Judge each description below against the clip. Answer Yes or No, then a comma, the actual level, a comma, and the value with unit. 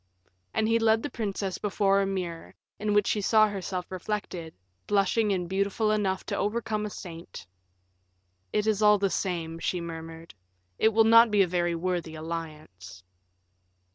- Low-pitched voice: No, high, 195 Hz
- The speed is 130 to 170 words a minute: Yes, average, 160 wpm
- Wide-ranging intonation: No, average, 3.8 semitones